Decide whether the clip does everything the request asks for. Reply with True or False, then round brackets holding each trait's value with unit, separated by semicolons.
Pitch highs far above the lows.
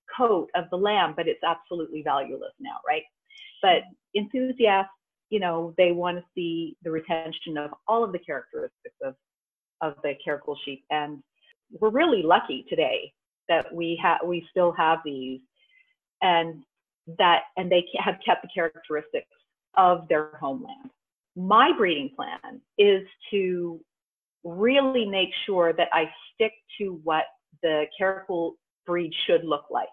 True (6.8 semitones)